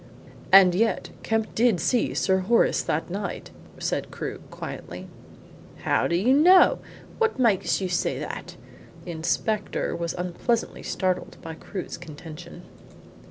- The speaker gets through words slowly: Yes, slow, 130 wpm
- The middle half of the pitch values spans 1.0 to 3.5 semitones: No, average, 4.8 semitones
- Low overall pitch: No, high, 190 Hz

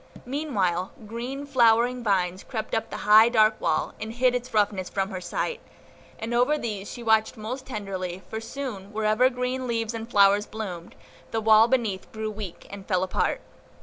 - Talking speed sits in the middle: Yes, average, 175 wpm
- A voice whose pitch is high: Yes, high, 220 Hz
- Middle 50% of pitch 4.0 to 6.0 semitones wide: No, average, 3.5 semitones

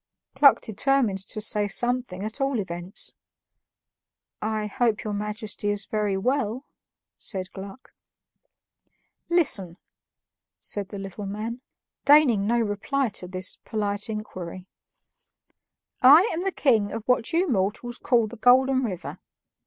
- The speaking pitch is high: Yes, high, 215 Hz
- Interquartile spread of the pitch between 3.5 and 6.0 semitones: Yes, average, 3.9 semitones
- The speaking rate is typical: No, slow, 125 wpm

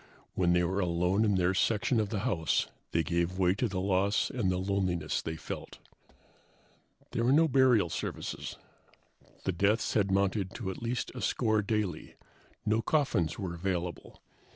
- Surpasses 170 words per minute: No, average, 165 wpm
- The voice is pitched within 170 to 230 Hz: No, very low, 95 Hz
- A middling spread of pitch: Yes, average, 3.6 semitones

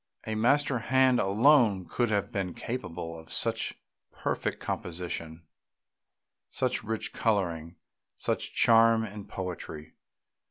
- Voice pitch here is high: No, low, 105 Hz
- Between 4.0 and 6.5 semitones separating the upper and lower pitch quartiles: Yes, average, 5.0 semitones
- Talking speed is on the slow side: Yes, slow, 110 wpm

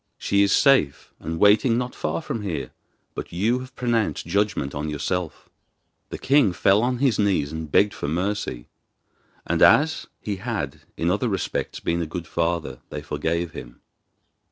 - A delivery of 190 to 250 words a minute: No, average, 170 wpm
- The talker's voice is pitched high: No, very low, 95 Hz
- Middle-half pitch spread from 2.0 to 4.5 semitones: No, wide, 5.5 semitones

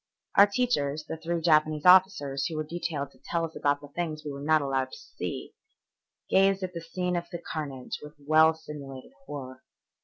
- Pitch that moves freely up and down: No, average, 3.2 semitones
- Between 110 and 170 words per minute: No, average, 180 wpm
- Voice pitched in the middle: Yes, medium, 155 Hz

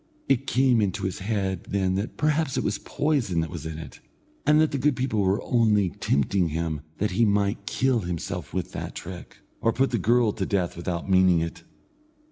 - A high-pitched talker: No, low, 100 Hz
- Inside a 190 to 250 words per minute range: Yes, average, 200 wpm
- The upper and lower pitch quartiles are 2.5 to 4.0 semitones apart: No, average, 5.2 semitones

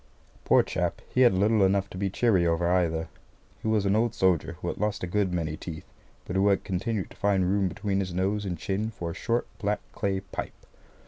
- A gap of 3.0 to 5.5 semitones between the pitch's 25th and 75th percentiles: No, narrow, 2.5 semitones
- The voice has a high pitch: No, very low, 95 Hz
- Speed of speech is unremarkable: No, fast, 220 wpm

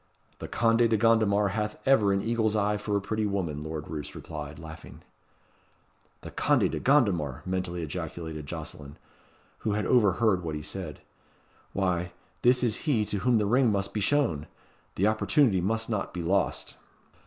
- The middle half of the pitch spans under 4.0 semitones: No, average, 4.7 semitones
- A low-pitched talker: Yes, low, 100 Hz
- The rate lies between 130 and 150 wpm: No, average, 165 wpm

